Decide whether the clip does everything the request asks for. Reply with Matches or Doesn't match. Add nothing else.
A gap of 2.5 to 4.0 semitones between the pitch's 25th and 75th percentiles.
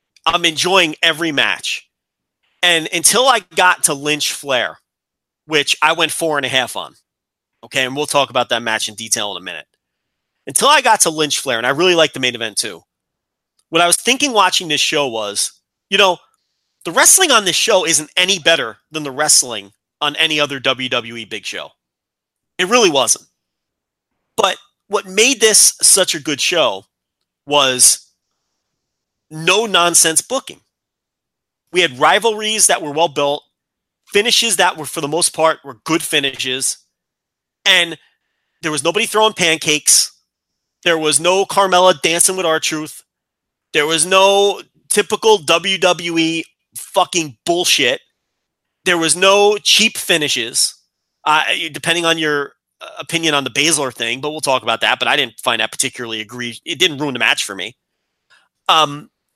Doesn't match